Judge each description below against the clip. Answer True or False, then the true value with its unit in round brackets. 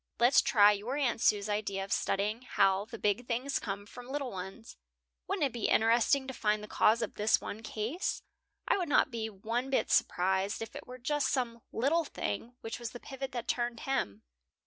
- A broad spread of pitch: False (3.6 semitones)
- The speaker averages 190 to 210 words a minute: True (200 wpm)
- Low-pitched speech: False (230 Hz)